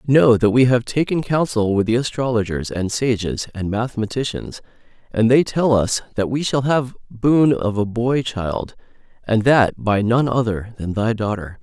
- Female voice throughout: No, male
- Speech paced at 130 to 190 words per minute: Yes, average, 175 wpm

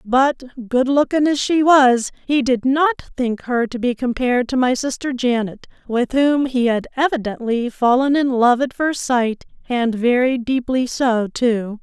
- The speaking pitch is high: Yes, very high, 255 Hz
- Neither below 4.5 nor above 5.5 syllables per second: No, 4.2 syllables/s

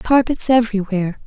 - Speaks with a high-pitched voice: Yes, high, 220 Hz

